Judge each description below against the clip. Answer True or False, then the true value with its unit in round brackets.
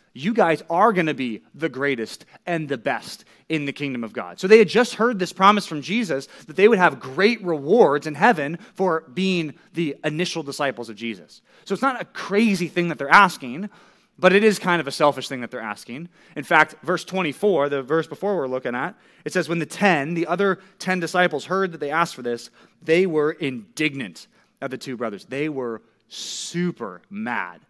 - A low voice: False (165 Hz)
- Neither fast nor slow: False (210 wpm)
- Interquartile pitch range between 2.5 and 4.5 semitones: False (5.1 semitones)